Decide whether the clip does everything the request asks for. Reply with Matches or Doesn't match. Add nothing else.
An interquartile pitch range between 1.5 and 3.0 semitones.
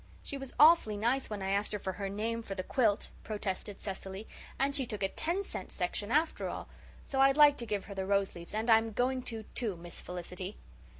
Doesn't match